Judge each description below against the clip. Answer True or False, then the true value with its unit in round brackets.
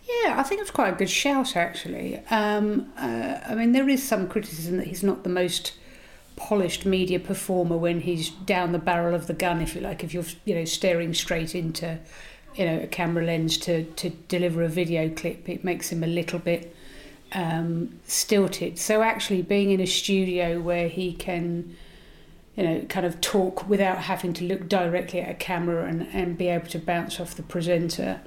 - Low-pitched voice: False (175 Hz)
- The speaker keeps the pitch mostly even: True (2.0 semitones)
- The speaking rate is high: False (195 wpm)